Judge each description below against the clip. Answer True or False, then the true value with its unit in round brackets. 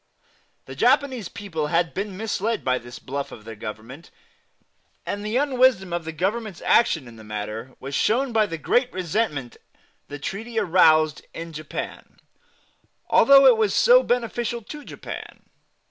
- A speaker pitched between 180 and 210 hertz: True (185 Hz)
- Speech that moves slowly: False (150 wpm)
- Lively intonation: True (8.4 semitones)